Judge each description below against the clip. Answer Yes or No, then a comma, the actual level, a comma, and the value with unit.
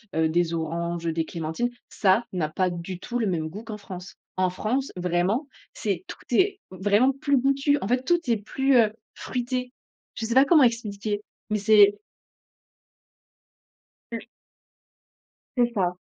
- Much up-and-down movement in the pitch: Yes, wide, 5.7 semitones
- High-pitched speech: Yes, high, 210 Hz